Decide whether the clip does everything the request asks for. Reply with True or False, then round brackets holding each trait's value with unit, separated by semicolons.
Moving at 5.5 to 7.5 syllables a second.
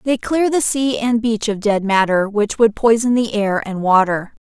False (4.5 syllables/s)